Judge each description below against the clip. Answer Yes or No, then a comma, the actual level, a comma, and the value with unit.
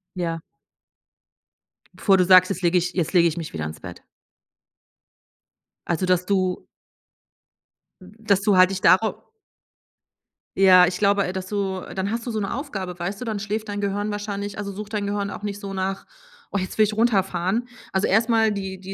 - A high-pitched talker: Yes, high, 195 Hz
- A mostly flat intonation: Yes, narrow, 2.0 semitones